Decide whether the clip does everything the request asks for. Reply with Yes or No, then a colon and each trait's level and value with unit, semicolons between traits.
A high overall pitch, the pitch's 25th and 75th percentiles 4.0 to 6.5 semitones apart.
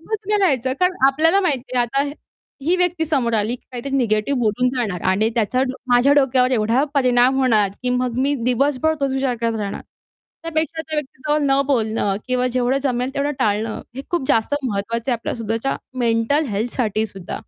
No: very high, 255 Hz; average, 3.6 semitones